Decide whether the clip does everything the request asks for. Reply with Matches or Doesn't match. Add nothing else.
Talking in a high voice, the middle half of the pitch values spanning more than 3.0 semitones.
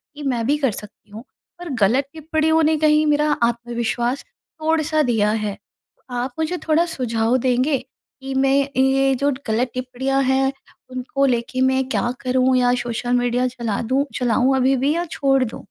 Doesn't match